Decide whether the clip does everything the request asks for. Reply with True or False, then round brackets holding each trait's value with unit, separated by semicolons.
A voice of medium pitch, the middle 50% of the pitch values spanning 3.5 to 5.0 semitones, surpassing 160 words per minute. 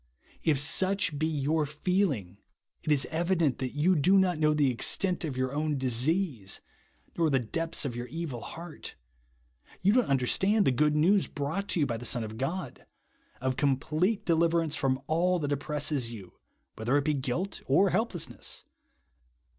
True (150 Hz; 4.7 semitones; 170 wpm)